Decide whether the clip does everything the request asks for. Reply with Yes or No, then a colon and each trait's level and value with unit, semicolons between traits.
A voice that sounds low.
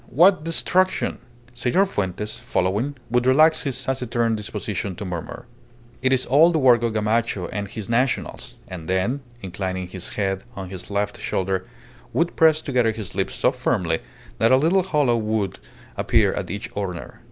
Yes: low, 115 Hz